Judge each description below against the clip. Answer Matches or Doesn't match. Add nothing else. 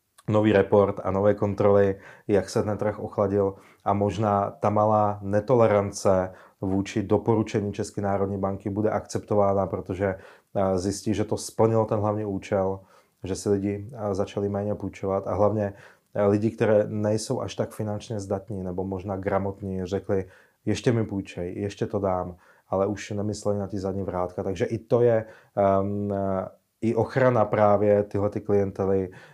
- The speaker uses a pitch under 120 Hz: Matches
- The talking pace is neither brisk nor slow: Matches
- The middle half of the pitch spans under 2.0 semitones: Matches